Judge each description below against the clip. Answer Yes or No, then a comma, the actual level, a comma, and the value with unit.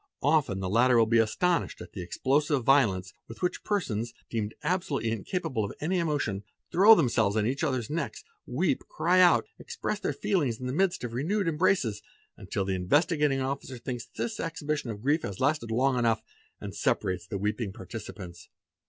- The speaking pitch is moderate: No, low, 130 Hz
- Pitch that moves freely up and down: Yes, wide, 6.8 semitones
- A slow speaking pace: No, average, 175 wpm